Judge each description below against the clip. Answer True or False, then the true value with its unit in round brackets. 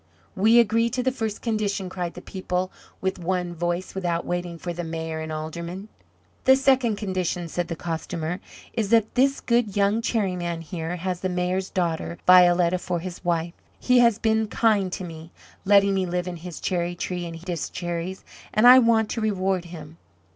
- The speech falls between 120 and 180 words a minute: False (190 wpm)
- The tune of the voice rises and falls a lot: False (3.6 semitones)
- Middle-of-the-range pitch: True (180 Hz)